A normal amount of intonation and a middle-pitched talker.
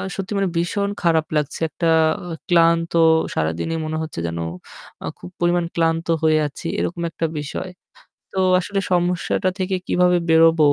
No: narrow, 2.0 semitones; medium, 165 Hz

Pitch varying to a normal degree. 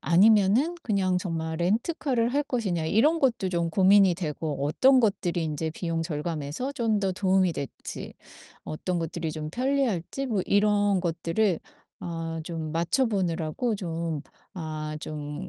Yes: average, 4.9 semitones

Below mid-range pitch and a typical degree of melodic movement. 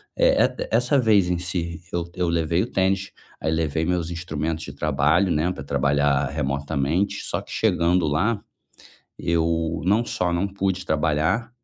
Yes: very low, 85 Hz; average, 3.4 semitones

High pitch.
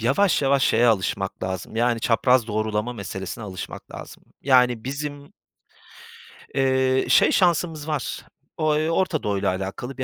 No: low, 125 Hz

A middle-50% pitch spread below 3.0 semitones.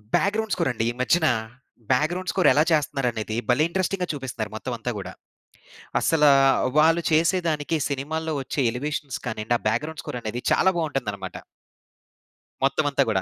No: average, 4.9 semitones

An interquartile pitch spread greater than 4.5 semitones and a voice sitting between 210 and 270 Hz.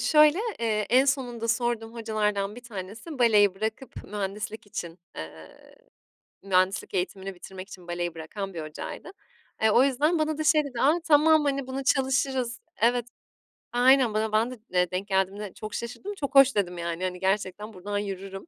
Yes: average, 5.2 semitones; high, 215 Hz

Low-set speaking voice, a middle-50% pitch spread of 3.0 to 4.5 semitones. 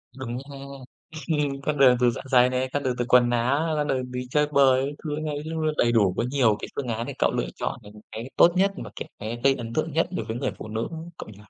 Yes: low, 130 Hz; average, 3.7 semitones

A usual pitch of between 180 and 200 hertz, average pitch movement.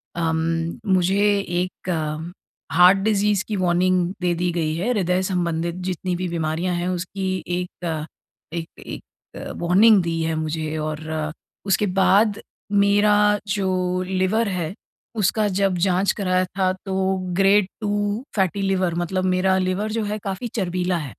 No: medium, 185 Hz; narrow, 2.2 semitones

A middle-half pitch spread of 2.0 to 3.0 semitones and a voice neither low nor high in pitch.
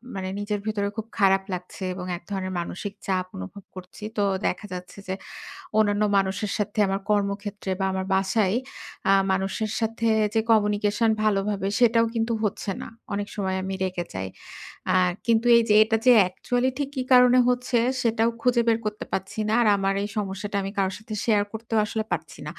No: average, 2.7 semitones; high, 205 Hz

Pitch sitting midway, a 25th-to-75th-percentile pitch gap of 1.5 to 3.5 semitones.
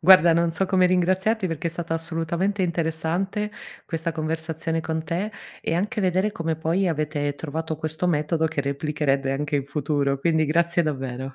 Yes: medium, 160 Hz; narrow, 2.5 semitones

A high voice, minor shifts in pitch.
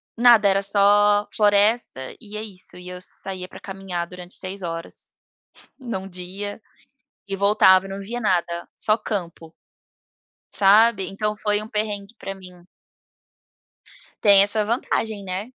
Yes: high, 200 Hz; narrow, 2.3 semitones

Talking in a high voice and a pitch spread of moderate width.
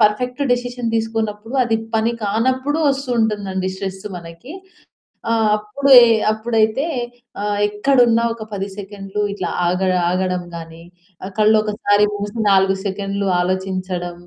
Yes: high, 210 Hz; average, 3.1 semitones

